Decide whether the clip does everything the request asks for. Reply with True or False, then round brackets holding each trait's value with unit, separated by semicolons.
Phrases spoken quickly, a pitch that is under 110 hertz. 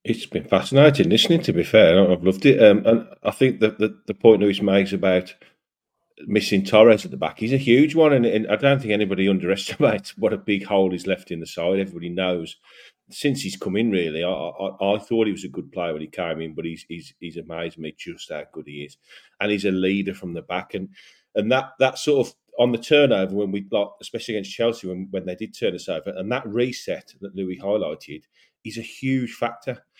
True (230 wpm; 100 Hz)